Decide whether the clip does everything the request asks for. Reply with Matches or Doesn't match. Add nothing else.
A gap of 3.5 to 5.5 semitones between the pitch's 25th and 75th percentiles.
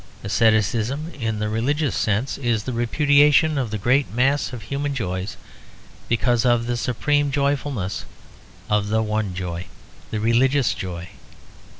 Matches